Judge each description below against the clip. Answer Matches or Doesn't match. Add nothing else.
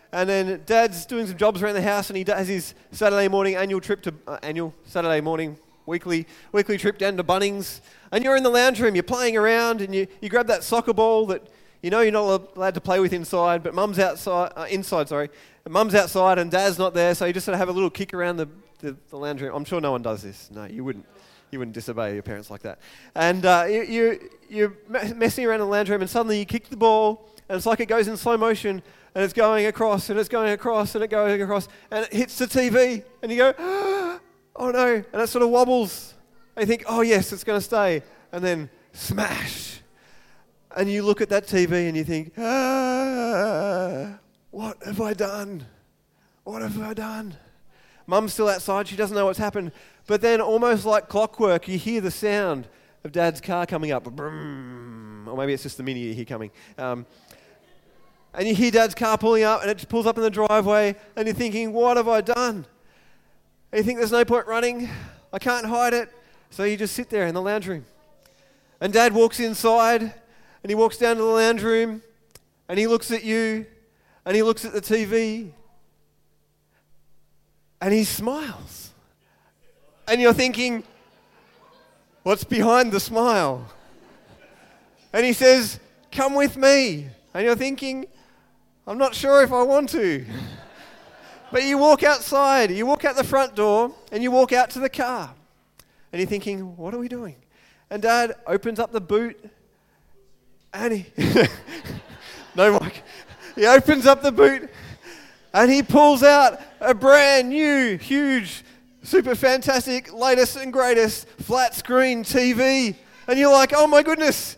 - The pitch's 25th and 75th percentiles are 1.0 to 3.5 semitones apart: Doesn't match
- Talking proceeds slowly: Doesn't match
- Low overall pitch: Doesn't match